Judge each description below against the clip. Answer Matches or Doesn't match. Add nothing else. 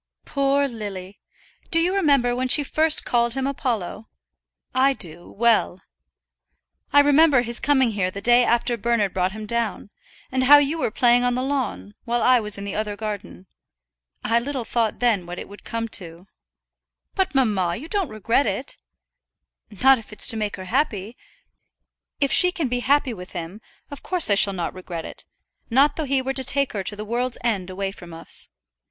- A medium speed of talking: Matches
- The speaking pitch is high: Matches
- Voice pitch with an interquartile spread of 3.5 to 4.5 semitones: Doesn't match